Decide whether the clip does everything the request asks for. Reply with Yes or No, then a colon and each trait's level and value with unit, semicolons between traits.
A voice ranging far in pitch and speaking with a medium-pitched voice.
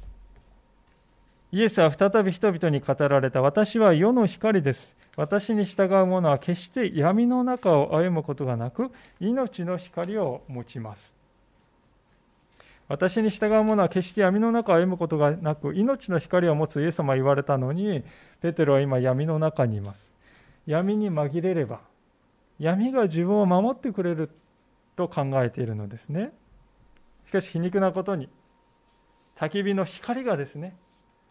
Yes: wide, 6.0 semitones; medium, 175 Hz